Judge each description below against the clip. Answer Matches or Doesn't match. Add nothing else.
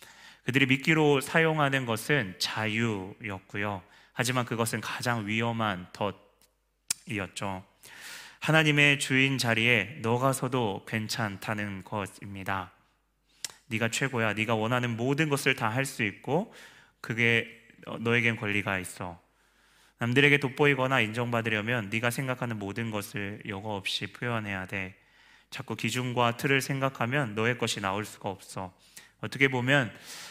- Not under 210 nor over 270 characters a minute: Doesn't match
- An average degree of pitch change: Matches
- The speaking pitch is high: Doesn't match